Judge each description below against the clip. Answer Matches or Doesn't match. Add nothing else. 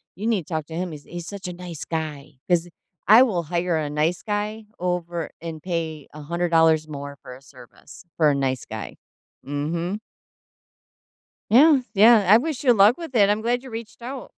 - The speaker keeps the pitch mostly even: Doesn't match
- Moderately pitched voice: Matches